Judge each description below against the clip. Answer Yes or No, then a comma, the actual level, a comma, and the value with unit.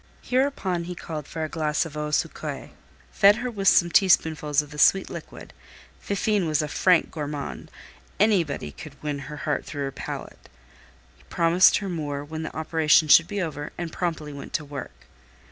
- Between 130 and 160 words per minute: No, average, 175 wpm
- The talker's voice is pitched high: No, medium, 160 Hz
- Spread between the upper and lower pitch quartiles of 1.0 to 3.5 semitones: Yes, average, 3.2 semitones